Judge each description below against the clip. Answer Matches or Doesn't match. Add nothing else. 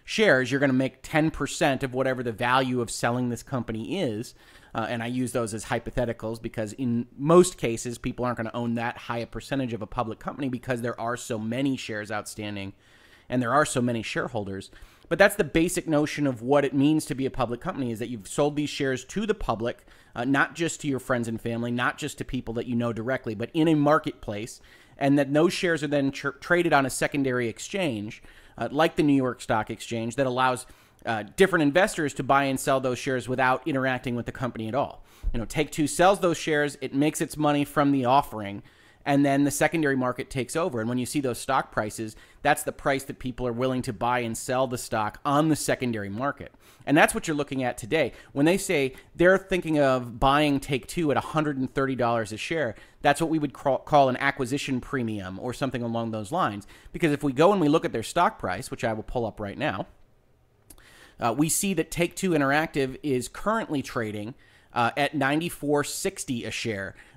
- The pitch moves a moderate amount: Matches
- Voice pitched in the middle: Doesn't match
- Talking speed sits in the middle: Doesn't match